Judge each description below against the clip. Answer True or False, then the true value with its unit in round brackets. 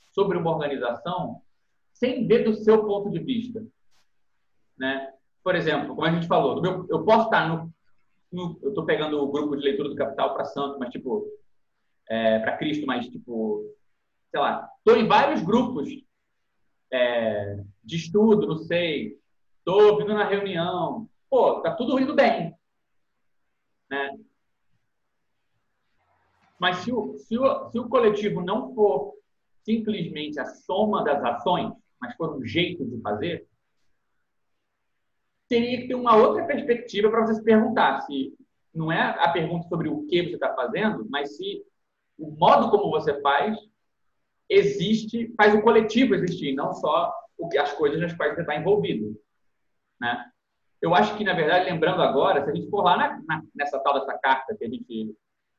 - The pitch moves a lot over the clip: True (8.1 semitones)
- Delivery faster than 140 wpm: True (160 wpm)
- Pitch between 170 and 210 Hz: True (190 Hz)